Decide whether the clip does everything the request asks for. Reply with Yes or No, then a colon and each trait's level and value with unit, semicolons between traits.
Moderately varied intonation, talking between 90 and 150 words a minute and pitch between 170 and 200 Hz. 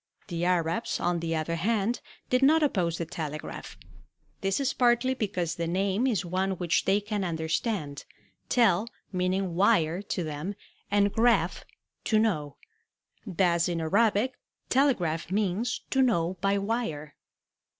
Yes: average, 4.9 semitones; average, 140 wpm; high, 190 Hz